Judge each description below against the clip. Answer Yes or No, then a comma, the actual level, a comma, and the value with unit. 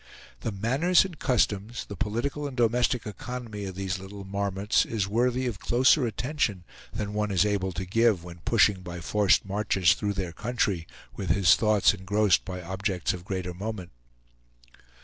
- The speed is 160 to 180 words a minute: Yes, average, 165 wpm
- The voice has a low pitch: Yes, low, 105 Hz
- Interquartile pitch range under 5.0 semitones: Yes, average, 3.6 semitones